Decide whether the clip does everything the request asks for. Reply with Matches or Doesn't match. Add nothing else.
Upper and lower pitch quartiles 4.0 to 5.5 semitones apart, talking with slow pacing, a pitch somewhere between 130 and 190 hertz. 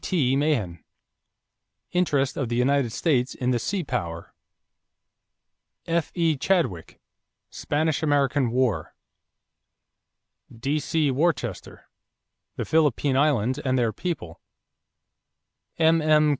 Matches